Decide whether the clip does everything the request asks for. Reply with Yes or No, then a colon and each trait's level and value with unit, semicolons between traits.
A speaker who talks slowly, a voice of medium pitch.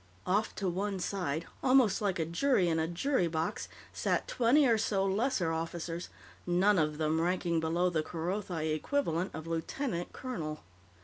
No: average, 160 wpm; medium, 175 Hz